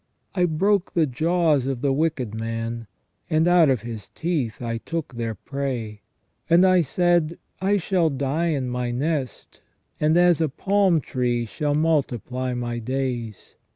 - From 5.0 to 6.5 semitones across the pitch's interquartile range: Yes, wide, 5.6 semitones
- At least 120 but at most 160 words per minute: Yes, average, 155 wpm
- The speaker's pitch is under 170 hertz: Yes, medium, 140 Hz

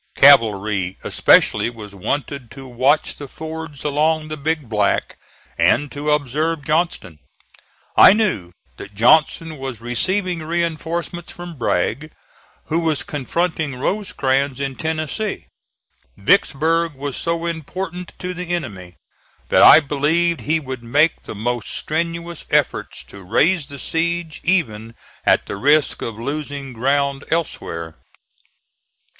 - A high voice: No, medium, 150 Hz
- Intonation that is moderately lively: Yes, average, 4.8 semitones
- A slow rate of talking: Yes, slow, 125 wpm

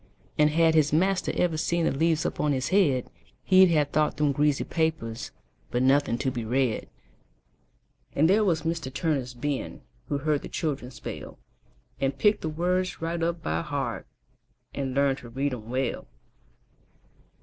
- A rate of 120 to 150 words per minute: No, average, 165 wpm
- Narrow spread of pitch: No, average, 3.8 semitones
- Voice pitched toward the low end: No, medium, 150 Hz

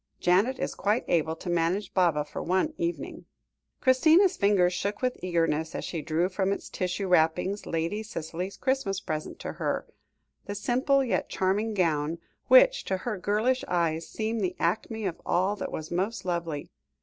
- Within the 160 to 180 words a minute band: Yes, average, 165 wpm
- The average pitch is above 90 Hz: Yes, high, 190 Hz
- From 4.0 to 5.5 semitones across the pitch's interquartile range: Yes, average, 4.6 semitones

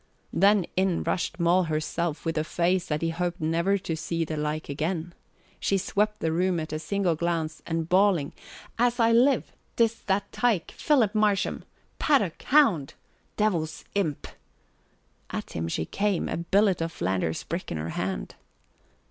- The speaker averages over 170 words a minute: No, average, 165 wpm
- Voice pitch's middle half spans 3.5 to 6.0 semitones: Yes, average, 4.0 semitones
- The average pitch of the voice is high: No, medium, 175 Hz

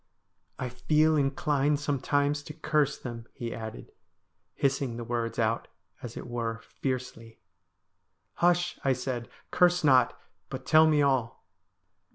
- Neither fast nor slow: Yes, average, 145 wpm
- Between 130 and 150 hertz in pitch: Yes, low, 135 Hz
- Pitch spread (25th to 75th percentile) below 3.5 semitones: No, average, 4.0 semitones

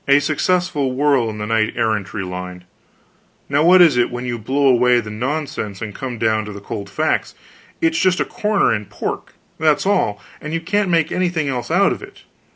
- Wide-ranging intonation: Yes, wide, 7.1 semitones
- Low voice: Yes, low, 130 Hz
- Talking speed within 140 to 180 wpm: No, average, 200 wpm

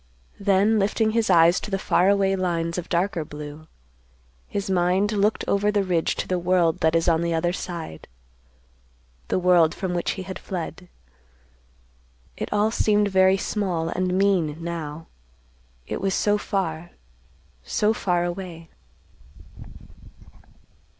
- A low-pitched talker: No, medium, 180 Hz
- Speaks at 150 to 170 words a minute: No, slow, 135 wpm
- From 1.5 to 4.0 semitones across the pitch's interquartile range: Yes, average, 3.0 semitones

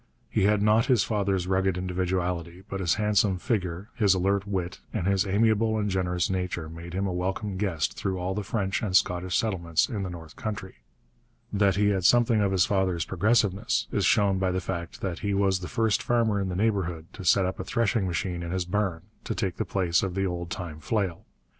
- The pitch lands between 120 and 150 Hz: No, very low, 95 Hz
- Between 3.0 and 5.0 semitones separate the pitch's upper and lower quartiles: No, narrow, 2.5 semitones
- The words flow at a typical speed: No, fast, 210 wpm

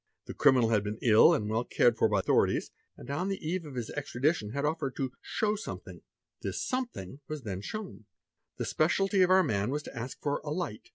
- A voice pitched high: No, medium, 140 Hz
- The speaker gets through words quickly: Yes, fast, 230 wpm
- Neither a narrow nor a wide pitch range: No, wide, 7.7 semitones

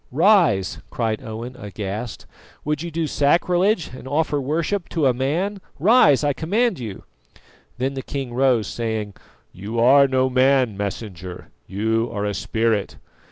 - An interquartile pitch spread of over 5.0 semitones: Yes, wide, 5.5 semitones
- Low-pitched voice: Yes, low, 130 Hz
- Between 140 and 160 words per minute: Yes, average, 145 wpm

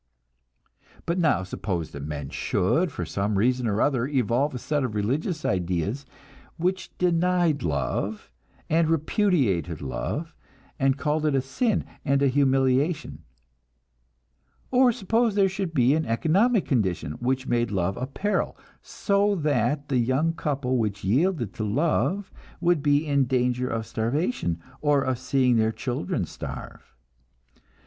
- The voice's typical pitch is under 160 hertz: Yes, low, 135 Hz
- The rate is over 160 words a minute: No, average, 140 wpm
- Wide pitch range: Yes, wide, 6.5 semitones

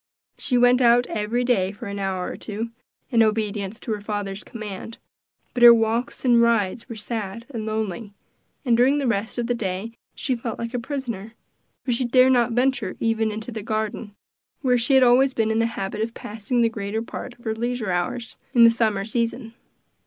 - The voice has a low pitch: No, high, 230 Hz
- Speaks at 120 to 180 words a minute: No, average, 200 wpm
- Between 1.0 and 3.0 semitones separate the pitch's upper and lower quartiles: Yes, narrow, 2.4 semitones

